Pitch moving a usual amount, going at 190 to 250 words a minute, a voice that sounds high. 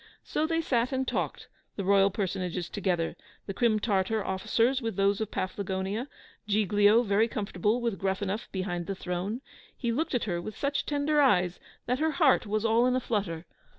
No: average, 4.0 semitones; average, 180 wpm; high, 210 Hz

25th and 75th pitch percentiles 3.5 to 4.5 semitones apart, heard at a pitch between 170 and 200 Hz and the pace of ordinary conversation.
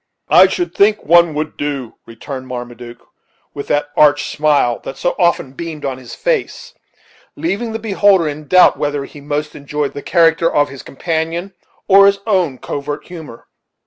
No: average, 4.1 semitones; medium, 150 Hz; average, 165 wpm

